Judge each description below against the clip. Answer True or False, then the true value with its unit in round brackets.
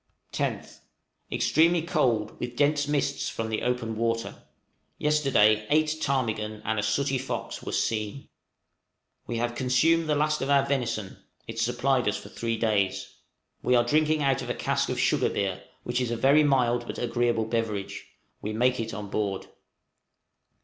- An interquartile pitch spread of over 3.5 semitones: True (4.0 semitones)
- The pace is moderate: True (160 wpm)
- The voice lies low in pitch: True (120 Hz)